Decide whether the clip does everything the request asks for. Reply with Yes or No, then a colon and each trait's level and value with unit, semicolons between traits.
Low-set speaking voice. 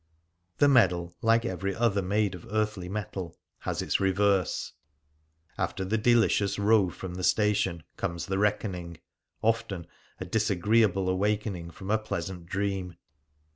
Yes: low, 100 Hz